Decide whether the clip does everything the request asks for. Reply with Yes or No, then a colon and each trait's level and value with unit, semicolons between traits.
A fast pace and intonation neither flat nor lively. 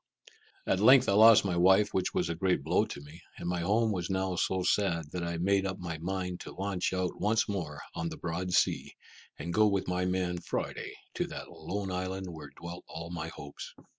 No: fast, 215 wpm; narrow, 2.2 semitones